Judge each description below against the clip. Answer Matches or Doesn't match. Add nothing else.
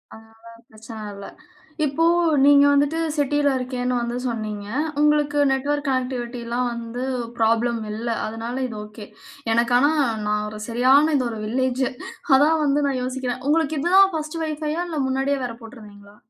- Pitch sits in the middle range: Doesn't match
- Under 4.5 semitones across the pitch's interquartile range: Matches